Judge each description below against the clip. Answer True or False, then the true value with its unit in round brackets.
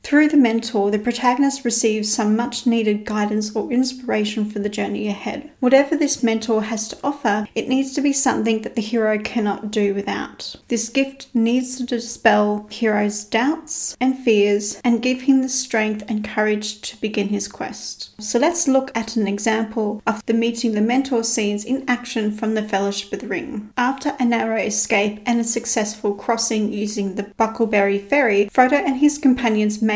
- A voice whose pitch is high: True (225 Hz)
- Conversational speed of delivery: True (180 wpm)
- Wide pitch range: False (3.0 semitones)